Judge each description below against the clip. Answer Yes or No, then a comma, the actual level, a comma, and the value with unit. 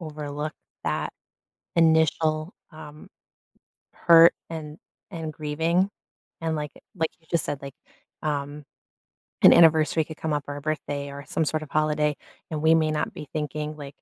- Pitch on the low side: No, medium, 155 Hz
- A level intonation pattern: Yes, narrow, 1.4 semitones